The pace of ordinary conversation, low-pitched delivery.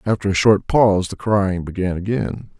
Yes: average, 185 wpm; low, 100 Hz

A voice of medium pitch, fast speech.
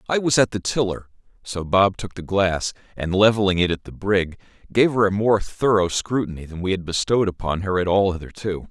No: very low, 95 Hz; fast, 215 wpm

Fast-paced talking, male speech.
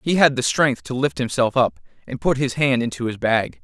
Yes: fast, 250 wpm; male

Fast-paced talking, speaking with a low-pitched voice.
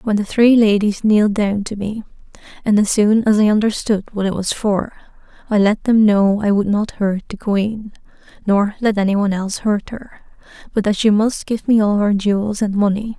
No: fast, 210 wpm; high, 210 Hz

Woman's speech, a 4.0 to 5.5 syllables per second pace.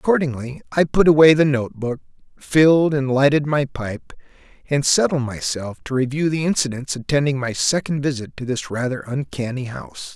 No: male; 5.3 syllables/s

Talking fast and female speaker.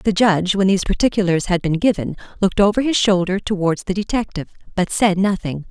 No: average, 190 wpm; female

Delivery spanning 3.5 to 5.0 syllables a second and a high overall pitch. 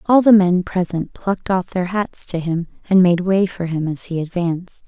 No: 4.9 syllables/s; medium, 180 Hz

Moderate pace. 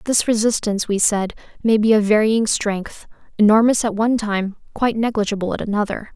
Yes: average, 165 wpm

